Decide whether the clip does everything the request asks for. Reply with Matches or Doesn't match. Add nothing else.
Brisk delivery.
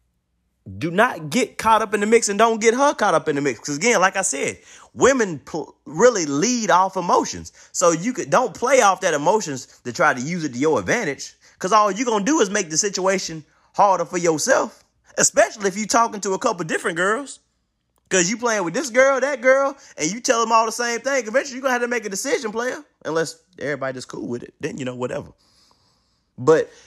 Matches